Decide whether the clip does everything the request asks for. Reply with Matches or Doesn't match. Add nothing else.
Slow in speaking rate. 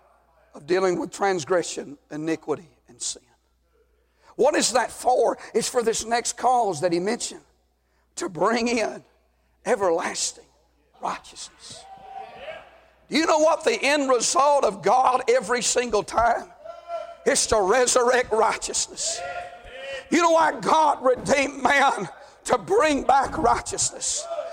Matches